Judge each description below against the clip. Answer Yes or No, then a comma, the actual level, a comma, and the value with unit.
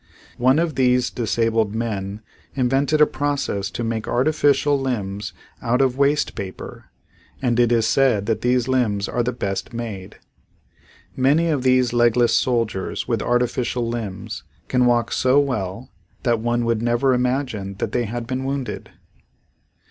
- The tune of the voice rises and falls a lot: No, narrow, 2.6 semitones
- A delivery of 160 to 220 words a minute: No, average, 150 wpm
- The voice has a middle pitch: No, low, 120 Hz